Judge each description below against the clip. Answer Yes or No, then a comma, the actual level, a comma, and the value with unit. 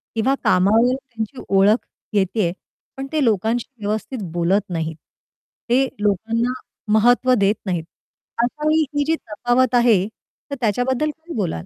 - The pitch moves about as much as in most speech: Yes, average, 4.3 semitones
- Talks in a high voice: Yes, high, 225 Hz